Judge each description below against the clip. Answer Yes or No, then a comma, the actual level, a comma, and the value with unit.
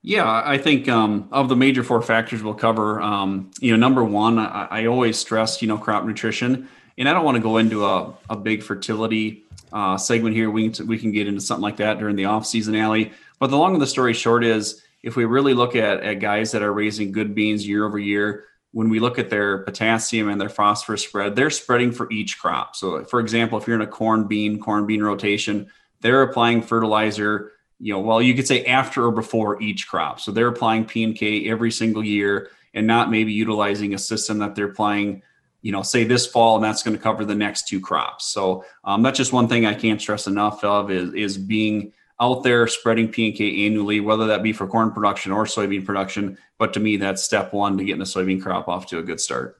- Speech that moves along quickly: Yes, fast, 235 wpm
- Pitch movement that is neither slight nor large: No, narrow, 1.7 semitones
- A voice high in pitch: No, low, 110 Hz